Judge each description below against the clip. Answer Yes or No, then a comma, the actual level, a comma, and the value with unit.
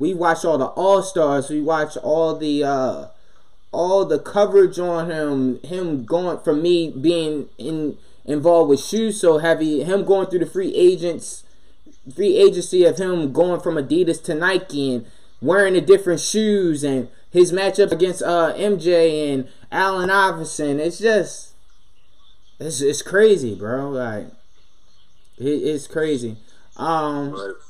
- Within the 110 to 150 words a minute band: Yes, average, 145 wpm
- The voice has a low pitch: No, medium, 165 Hz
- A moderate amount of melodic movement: Yes, average, 4.2 semitones